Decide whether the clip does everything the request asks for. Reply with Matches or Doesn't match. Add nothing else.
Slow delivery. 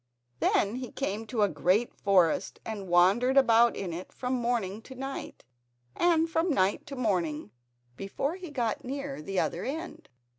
Doesn't match